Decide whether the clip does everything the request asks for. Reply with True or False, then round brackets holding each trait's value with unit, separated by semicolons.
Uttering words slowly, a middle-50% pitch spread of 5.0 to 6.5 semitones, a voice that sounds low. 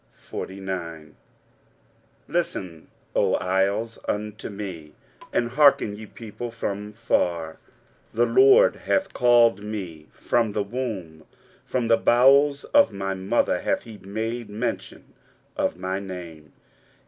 False (115 wpm; 4.1 semitones; 105 Hz)